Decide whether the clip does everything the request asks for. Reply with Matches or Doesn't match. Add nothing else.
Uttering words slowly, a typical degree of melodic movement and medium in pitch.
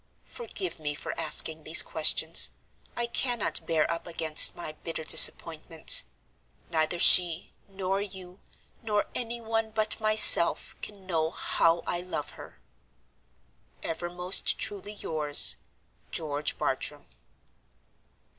Matches